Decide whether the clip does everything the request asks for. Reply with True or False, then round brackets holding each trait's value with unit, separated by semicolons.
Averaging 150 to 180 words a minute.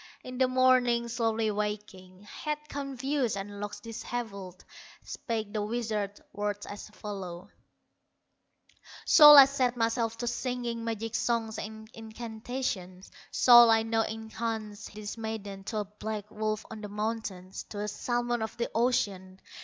False (140 wpm)